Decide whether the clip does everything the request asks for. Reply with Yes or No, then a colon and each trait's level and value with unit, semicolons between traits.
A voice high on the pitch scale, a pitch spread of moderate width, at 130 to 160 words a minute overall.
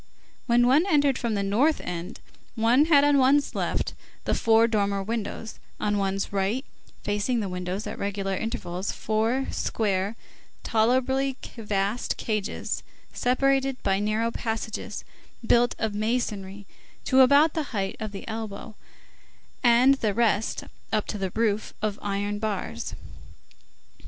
Yes: high, 220 Hz; average, 3.7 semitones; slow, 135 wpm